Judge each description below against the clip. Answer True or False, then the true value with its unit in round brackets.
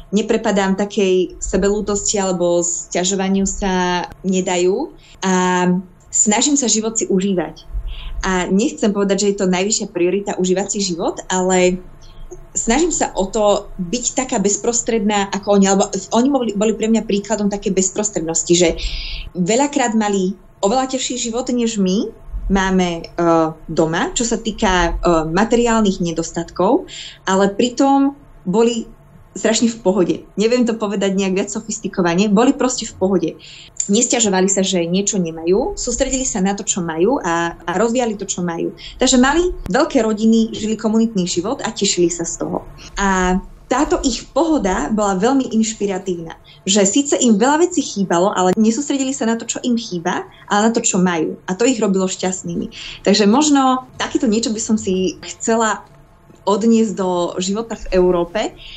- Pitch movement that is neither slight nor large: True (3.9 semitones)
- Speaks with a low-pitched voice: False (200 Hz)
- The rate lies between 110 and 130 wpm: False (150 wpm)